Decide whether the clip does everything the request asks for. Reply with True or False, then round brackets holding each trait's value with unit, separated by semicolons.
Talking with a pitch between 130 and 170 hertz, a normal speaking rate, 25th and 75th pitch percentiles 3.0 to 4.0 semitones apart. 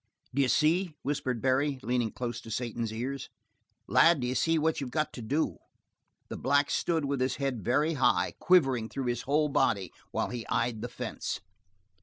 True (135 Hz; 175 wpm; 3.6 semitones)